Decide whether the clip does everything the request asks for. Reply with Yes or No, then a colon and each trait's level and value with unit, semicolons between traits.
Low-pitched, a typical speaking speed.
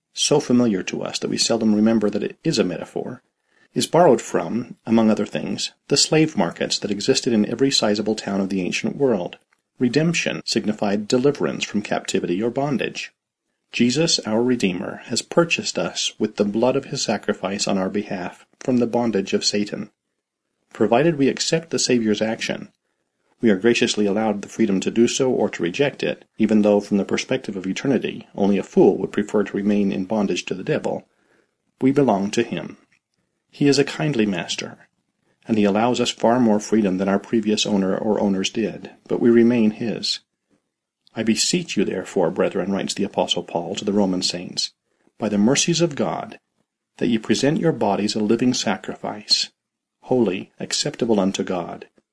Yes: low, 110 Hz; average, 175 wpm